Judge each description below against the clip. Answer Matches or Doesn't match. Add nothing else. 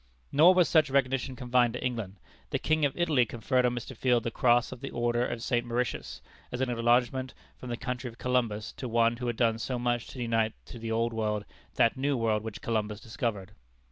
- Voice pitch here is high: Doesn't match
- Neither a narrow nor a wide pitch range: Doesn't match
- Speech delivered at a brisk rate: Matches